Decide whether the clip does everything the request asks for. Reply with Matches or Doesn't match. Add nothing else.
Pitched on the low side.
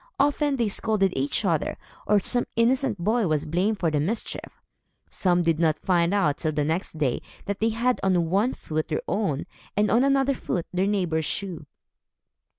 Doesn't match